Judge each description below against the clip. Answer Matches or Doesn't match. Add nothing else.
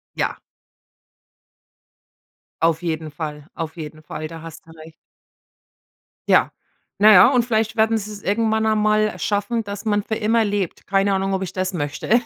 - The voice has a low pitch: Doesn't match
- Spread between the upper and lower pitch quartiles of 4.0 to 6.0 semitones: Matches